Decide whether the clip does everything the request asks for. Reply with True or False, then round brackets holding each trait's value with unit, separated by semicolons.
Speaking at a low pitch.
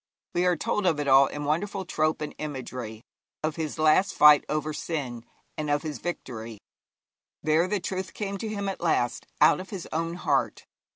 False (155 Hz)